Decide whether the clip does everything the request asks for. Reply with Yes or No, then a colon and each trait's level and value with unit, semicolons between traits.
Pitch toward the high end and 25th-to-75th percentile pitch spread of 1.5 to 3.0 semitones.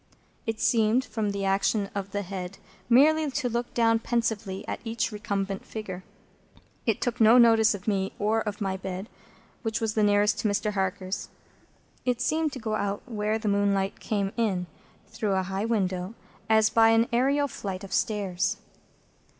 Yes: high, 210 Hz; narrow, 2.6 semitones